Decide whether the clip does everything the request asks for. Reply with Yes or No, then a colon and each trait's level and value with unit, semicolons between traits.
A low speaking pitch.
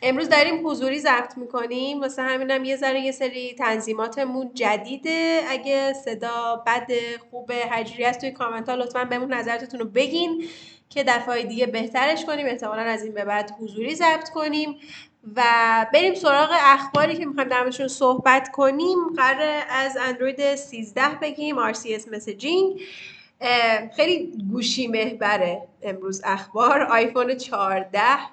No: very high, 255 Hz